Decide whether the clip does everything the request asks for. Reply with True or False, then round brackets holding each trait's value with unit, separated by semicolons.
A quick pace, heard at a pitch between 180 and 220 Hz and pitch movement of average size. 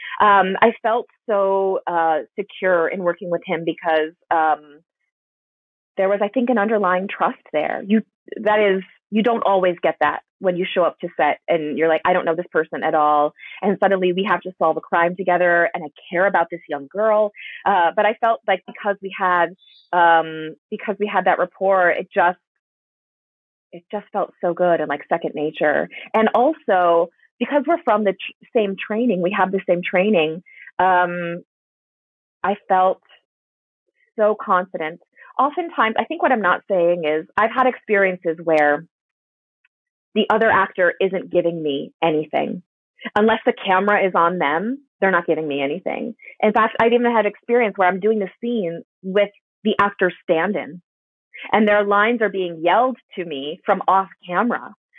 False (170 wpm; 185 Hz; 3.8 semitones)